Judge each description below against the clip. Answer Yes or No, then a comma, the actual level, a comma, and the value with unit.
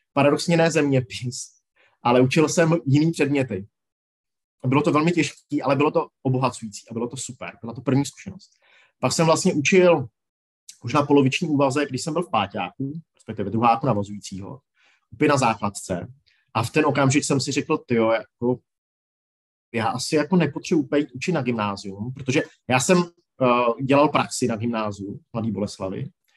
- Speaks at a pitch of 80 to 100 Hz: No, low, 135 Hz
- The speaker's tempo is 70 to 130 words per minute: No, average, 160 wpm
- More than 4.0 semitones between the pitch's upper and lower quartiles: Yes, average, 4.6 semitones